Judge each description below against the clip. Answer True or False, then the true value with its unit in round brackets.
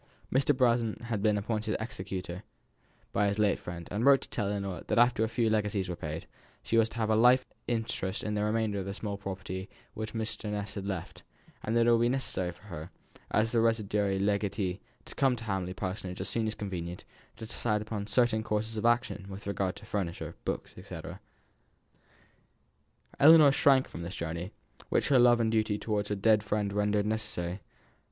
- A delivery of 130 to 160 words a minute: False (195 wpm)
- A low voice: True (105 Hz)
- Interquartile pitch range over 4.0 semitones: False (2.6 semitones)